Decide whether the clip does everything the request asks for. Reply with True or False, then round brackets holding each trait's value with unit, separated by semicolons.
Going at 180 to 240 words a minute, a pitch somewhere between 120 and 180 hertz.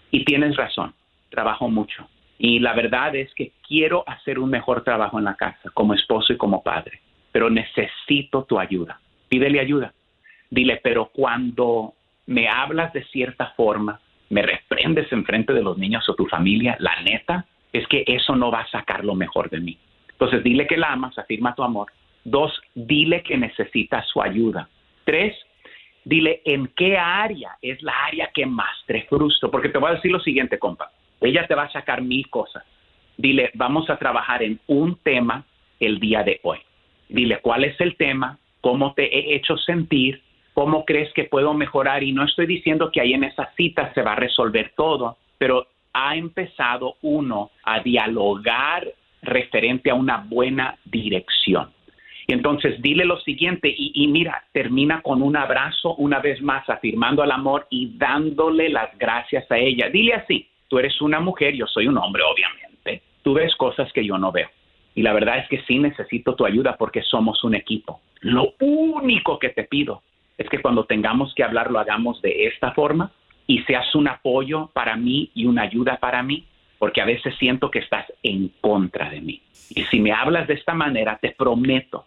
True (185 wpm; 135 Hz)